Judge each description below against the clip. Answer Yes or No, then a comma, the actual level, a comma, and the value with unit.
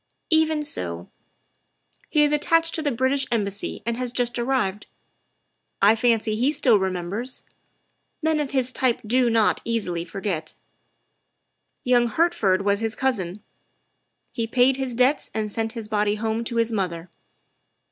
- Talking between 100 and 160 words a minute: Yes, average, 145 wpm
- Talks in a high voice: Yes, high, 230 Hz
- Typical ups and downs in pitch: Yes, average, 3.9 semitones